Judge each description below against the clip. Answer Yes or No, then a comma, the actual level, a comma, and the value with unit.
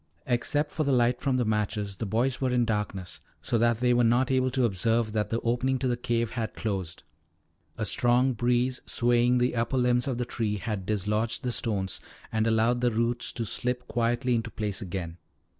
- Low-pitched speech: Yes, low, 120 Hz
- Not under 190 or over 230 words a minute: Yes, average, 200 wpm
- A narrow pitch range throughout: Yes, narrow, 2.3 semitones